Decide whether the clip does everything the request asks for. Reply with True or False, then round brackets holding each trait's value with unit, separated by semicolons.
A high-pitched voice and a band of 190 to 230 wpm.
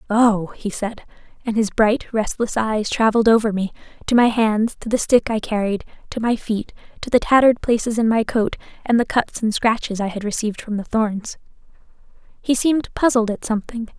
True (220 Hz; 195 wpm)